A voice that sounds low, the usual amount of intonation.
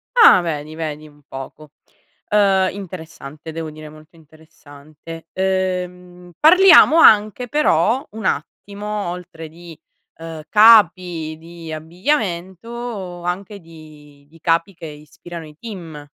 No: medium, 170 Hz; average, 3.9 semitones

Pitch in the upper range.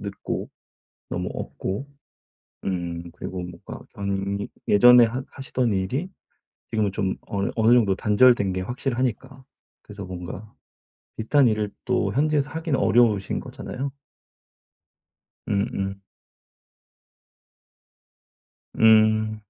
No: low, 110 Hz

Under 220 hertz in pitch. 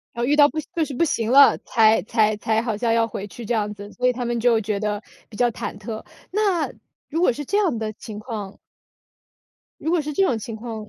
No: high, 230 Hz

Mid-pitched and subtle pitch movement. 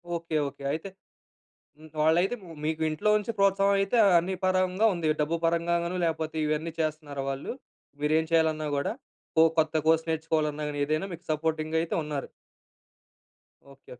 Yes: medium, 160 Hz; narrow, 1.9 semitones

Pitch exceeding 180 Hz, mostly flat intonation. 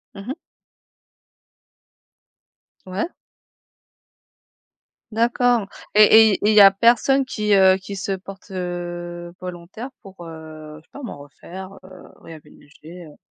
No: high, 190 Hz; average, 3.6 semitones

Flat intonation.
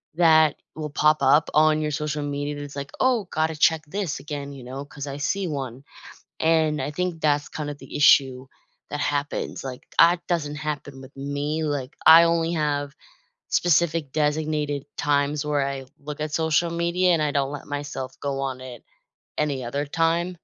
Yes: narrow, 2.0 semitones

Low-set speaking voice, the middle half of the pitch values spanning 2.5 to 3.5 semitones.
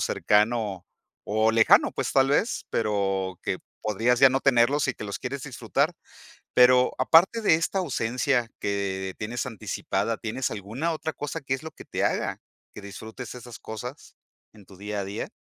No: low, 120 Hz; average, 4.4 semitones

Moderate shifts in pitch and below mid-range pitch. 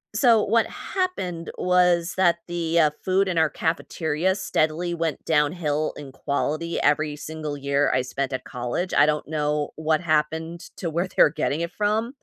No: average, 3.0 semitones; medium, 160 Hz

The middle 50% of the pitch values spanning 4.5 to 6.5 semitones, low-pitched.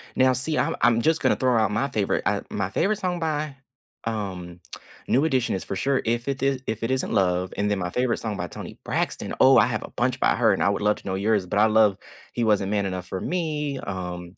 Yes: average, 5.1 semitones; low, 110 Hz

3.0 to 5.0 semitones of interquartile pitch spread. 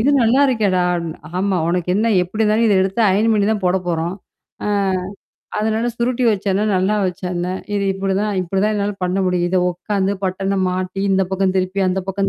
No: narrow, 2.4 semitones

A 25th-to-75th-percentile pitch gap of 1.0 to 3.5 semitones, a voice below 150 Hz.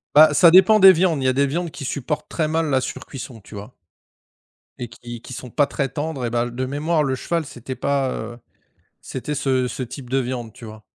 No: average, 3.9 semitones; low, 135 Hz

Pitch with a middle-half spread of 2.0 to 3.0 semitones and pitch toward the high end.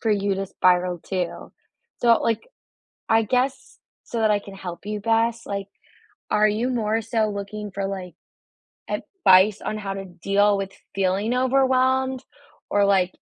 Yes: average, 2.7 semitones; high, 210 Hz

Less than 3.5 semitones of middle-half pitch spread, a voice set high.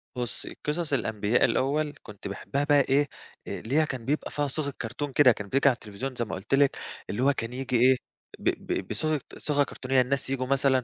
No: average, 2.8 semitones; low, 135 Hz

